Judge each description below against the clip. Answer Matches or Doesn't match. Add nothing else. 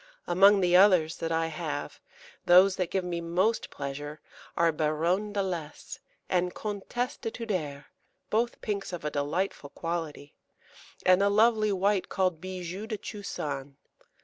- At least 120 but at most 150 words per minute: Matches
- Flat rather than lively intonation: Doesn't match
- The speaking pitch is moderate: Matches